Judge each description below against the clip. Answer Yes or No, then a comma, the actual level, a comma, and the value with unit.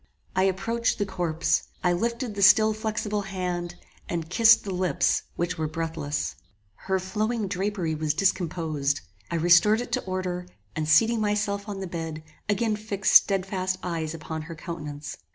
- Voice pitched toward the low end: No, medium, 185 Hz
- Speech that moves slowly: No, average, 155 wpm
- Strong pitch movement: No, average, 4.0 semitones